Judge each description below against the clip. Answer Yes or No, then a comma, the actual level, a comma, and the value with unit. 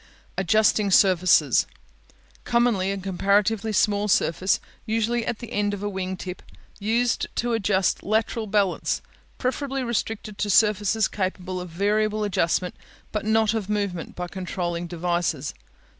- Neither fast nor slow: No, slow, 130 wpm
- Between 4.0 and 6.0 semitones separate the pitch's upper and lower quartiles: No, average, 2.9 semitones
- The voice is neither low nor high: No, high, 205 Hz